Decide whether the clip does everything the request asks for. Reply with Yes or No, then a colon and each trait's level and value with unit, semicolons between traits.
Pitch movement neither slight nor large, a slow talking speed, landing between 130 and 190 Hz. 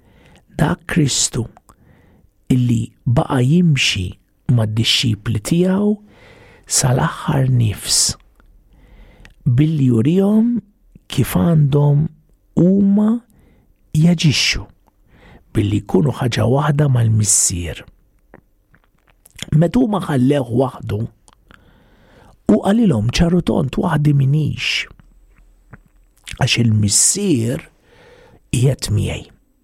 No: wide, 7.3 semitones; slow, 75 wpm; low, 135 Hz